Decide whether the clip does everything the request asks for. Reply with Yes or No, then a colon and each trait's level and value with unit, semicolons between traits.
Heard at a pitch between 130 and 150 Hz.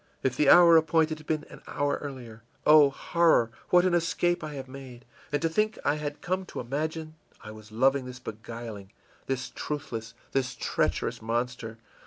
Yes: medium, 140 Hz